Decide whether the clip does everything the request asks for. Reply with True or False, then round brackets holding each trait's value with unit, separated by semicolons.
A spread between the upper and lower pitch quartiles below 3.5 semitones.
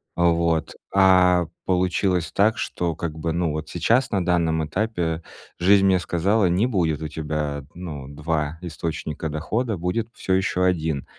True (2.9 semitones)